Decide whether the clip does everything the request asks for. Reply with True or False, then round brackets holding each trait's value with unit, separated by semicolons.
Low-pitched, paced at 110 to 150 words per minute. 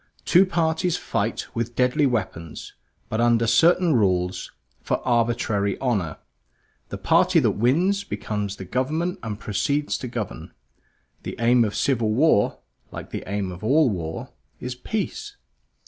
True (120 Hz; 140 wpm)